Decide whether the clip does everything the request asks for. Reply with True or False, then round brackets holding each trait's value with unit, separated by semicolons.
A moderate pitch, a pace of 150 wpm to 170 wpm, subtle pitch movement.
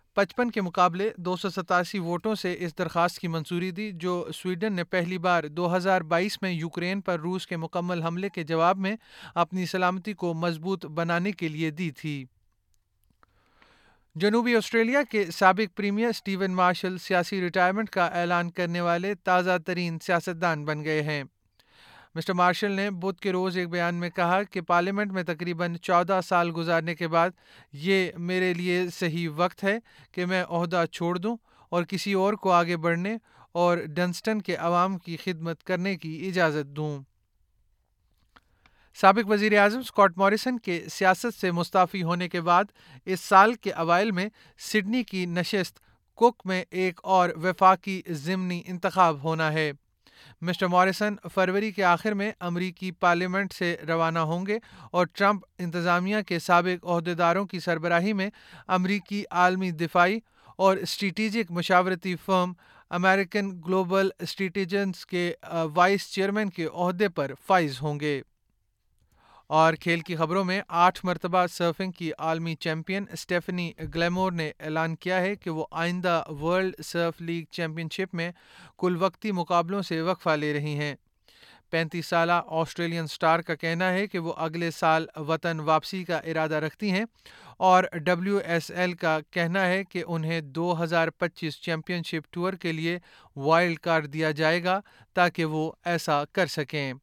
True (175 Hz; 155 wpm; 2.3 semitones)